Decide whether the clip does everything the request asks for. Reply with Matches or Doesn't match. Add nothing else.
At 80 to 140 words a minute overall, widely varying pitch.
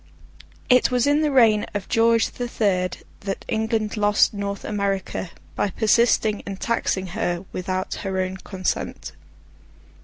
Doesn't match